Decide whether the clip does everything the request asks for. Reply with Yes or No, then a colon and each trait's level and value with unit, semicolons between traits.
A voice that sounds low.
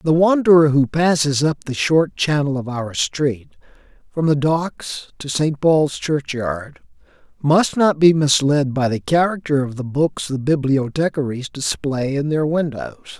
No: medium, 145 Hz